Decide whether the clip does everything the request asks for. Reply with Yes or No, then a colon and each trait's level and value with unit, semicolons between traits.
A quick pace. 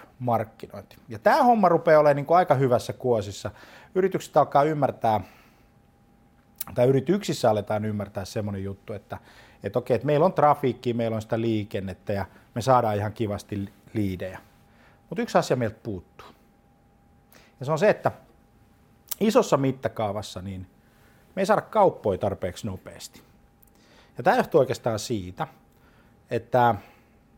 No: average, 135 wpm